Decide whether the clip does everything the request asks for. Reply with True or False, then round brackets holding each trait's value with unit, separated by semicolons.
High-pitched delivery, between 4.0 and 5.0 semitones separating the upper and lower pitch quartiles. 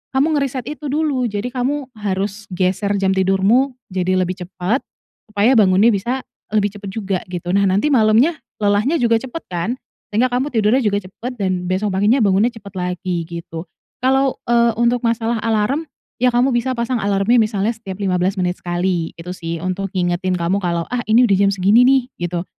True (205 Hz; 4.7 semitones)